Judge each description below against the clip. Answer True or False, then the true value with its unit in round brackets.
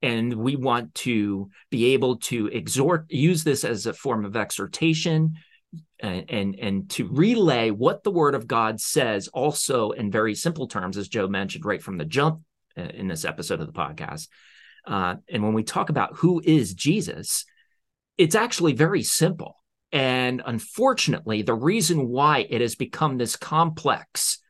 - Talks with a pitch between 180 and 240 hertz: False (130 Hz)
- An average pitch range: False (6.1 semitones)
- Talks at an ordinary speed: True (165 wpm)